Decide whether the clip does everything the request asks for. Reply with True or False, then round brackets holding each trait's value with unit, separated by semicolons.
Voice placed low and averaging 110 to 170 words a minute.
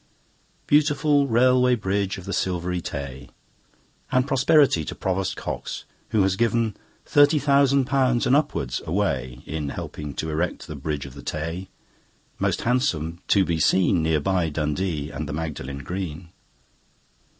True (95 Hz; 145 wpm)